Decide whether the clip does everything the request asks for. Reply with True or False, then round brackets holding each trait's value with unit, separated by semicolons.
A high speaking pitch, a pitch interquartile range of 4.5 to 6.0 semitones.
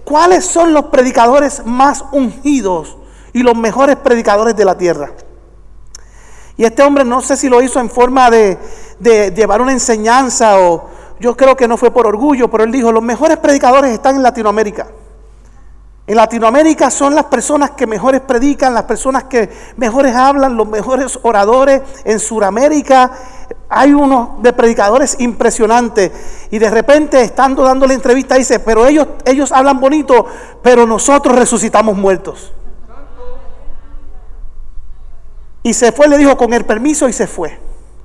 False (255 Hz; 3.3 semitones)